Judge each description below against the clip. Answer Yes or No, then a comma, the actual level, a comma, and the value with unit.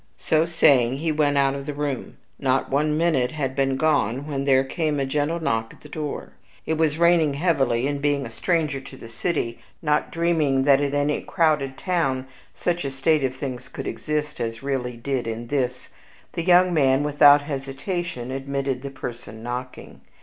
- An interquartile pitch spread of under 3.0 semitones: Yes, narrow, 2.6 semitones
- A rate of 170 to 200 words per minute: Yes, average, 185 wpm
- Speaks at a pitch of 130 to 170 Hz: Yes, medium, 140 Hz